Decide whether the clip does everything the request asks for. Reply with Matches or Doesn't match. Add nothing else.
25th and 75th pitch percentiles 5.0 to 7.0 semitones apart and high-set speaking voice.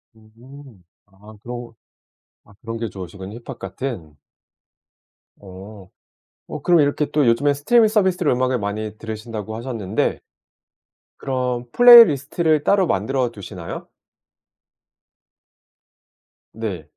Doesn't match